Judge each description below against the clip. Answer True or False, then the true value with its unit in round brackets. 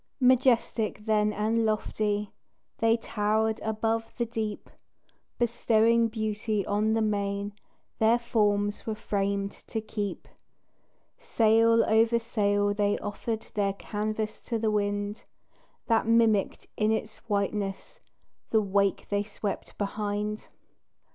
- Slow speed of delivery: True (115 wpm)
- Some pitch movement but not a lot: False (1.7 semitones)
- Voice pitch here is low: False (215 Hz)